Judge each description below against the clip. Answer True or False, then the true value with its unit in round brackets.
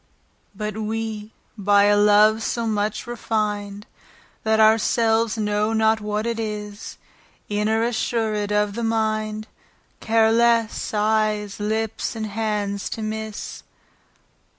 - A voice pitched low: False (215 Hz)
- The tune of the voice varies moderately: False (1.2 semitones)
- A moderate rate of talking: False (120 wpm)